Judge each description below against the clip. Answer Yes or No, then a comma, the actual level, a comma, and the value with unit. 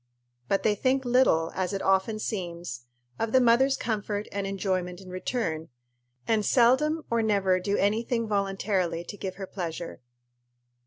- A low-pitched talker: No, high, 200 Hz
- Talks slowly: No, average, 155 wpm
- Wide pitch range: No, average, 3.8 semitones